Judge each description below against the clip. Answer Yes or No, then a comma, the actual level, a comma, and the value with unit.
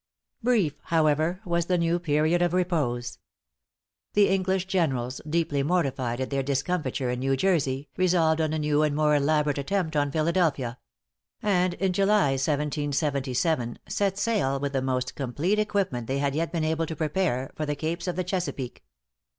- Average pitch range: Yes, average, 4.5 semitones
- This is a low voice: No, medium, 155 Hz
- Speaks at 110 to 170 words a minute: Yes, average, 165 wpm